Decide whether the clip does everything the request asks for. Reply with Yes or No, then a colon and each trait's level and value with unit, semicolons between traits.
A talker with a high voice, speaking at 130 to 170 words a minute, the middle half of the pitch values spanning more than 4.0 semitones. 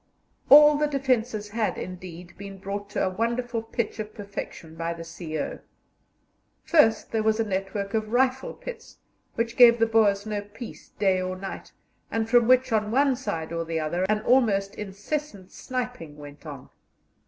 Yes: high, 210 Hz; average, 165 wpm; average, 4.4 semitones